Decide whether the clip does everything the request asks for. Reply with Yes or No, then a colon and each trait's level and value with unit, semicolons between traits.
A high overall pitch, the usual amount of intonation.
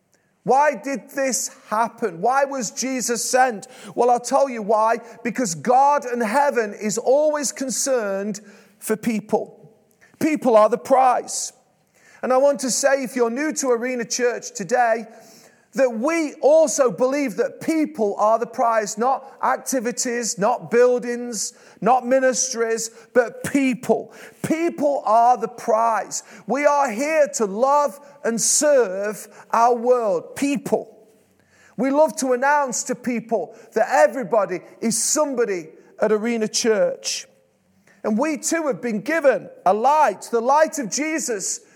Yes: high, 245 Hz; average, 3.6 semitones